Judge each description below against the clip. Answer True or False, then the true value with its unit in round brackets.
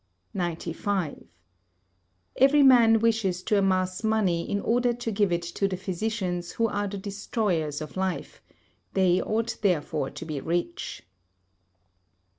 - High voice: True (195 Hz)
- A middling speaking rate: False (130 wpm)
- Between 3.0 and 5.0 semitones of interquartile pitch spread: True (4.0 semitones)